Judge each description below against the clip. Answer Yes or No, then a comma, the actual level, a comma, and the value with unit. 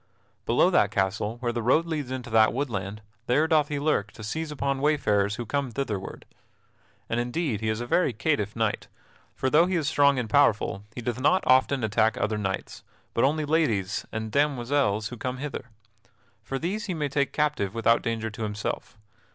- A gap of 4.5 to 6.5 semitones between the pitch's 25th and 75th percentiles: Yes, average, 5.0 semitones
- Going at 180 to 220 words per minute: Yes, average, 190 wpm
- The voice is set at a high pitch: No, low, 125 Hz